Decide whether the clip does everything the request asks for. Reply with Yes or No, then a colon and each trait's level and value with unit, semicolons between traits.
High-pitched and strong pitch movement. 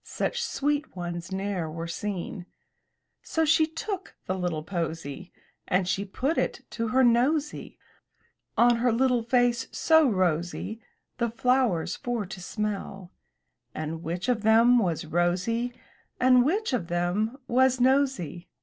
Yes: high, 220 Hz; wide, 6.2 semitones